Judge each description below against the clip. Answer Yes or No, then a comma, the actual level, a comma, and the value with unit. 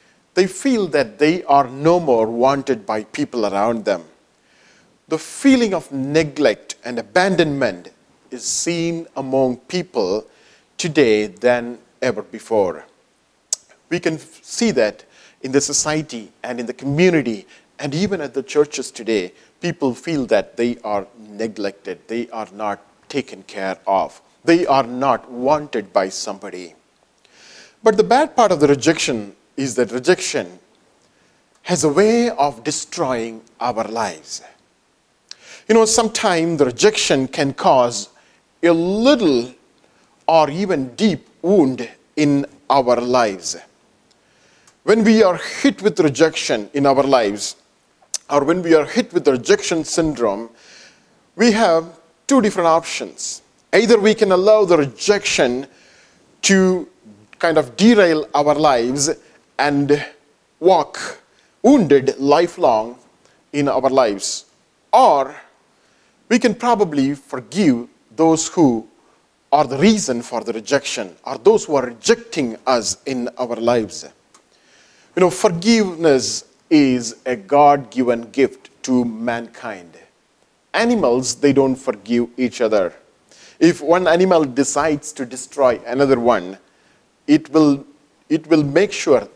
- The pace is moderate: No, slow, 125 wpm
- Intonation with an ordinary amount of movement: No, wide, 6.4 semitones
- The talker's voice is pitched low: No, medium, 145 Hz